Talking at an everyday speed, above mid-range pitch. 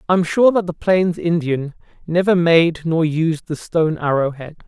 No: average, 195 wpm; medium, 165 Hz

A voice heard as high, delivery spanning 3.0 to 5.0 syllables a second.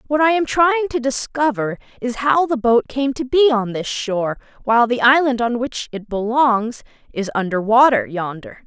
Yes: high, 245 Hz; 4.9 syllables/s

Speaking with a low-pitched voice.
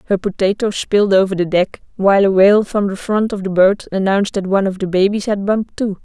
No: high, 195 Hz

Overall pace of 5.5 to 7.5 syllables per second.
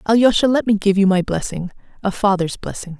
Yes: 5.9 syllables/s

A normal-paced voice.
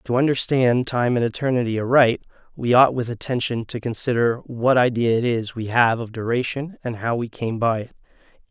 Yes: average, 185 wpm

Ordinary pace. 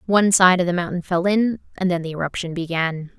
No: fast, 225 wpm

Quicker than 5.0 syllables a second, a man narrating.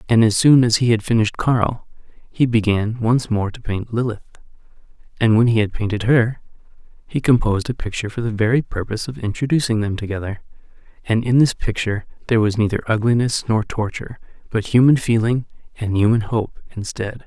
Yes: 5.8 syllables/s; male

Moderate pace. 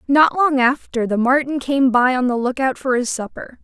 No: fast, 230 wpm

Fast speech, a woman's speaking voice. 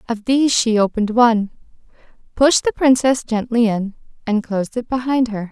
No: average, 165 wpm; female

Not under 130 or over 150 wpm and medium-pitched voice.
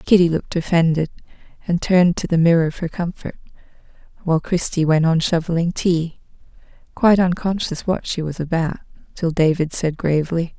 Yes: average, 145 wpm; medium, 170 Hz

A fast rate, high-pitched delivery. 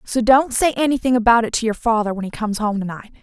Yes: fast, 280 wpm; high, 230 Hz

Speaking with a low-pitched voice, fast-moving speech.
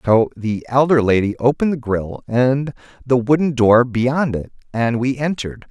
No: low, 125 Hz; average, 170 wpm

